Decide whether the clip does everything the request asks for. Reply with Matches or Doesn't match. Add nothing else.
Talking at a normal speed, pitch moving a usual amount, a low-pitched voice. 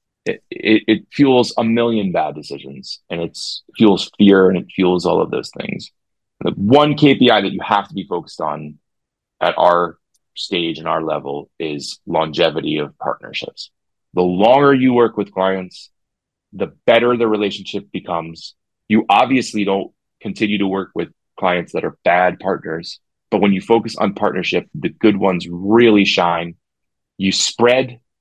Matches